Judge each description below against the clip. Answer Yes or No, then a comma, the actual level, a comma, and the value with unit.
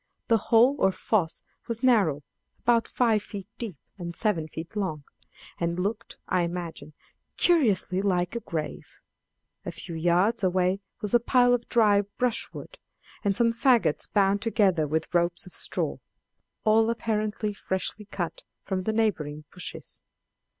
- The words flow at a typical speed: Yes, average, 145 wpm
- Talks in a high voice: Yes, high, 200 Hz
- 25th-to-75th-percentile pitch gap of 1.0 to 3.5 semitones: No, average, 4.6 semitones